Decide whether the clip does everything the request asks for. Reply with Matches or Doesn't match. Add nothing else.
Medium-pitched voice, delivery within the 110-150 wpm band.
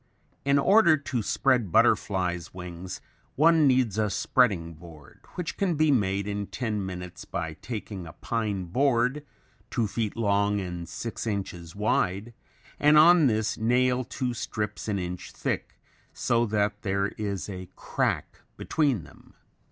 Doesn't match